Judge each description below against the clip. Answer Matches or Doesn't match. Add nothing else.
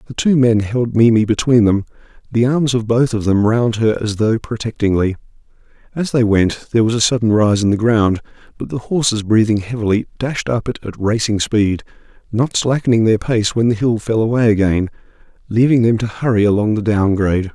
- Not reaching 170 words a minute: Doesn't match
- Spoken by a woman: Doesn't match